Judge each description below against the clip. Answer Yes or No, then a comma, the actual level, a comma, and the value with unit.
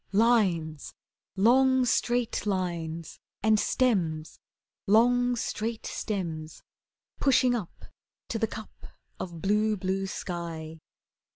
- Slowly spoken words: Yes, slow, 95 wpm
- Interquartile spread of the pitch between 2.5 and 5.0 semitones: No, wide, 5.6 semitones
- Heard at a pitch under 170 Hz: No, high, 205 Hz